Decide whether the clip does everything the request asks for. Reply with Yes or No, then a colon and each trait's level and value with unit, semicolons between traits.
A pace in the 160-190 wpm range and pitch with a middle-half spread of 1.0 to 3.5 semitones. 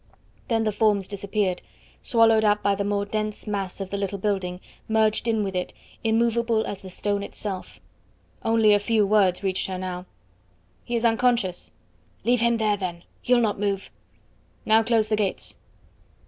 Yes: average, 165 wpm; narrow, 2.4 semitones